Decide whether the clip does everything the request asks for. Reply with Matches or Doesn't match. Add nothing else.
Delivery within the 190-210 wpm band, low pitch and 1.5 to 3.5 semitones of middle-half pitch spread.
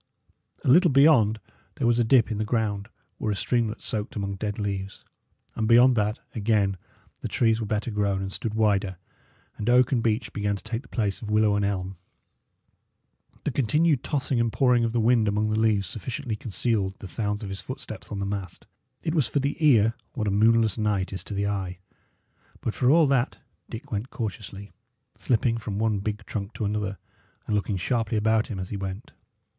Matches